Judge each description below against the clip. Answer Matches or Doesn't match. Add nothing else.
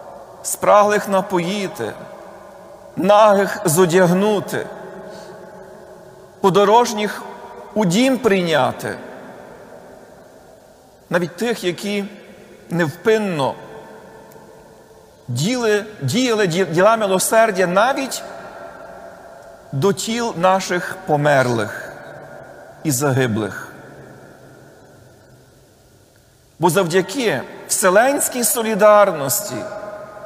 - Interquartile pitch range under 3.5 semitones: Matches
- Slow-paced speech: Matches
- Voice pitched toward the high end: Matches